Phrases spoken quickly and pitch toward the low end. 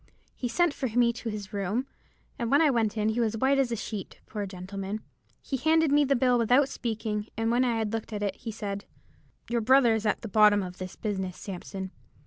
No: fast, 230 wpm; high, 225 Hz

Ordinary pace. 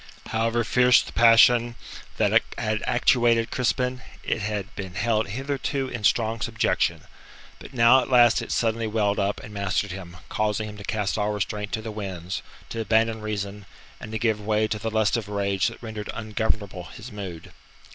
Yes: average, 175 wpm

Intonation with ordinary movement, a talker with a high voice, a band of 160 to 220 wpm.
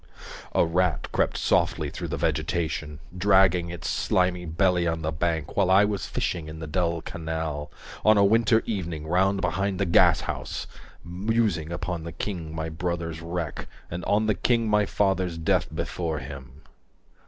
No: average, 3.2 semitones; very low, 85 Hz; average, 165 wpm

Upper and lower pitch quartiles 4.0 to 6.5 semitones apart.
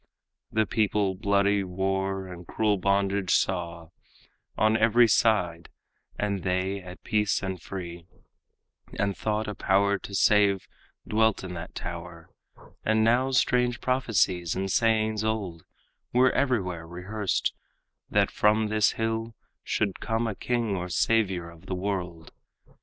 No: average, 3.2 semitones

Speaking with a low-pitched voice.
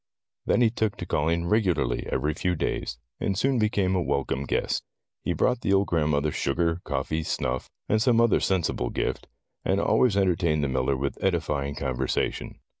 Yes: very low, 85 Hz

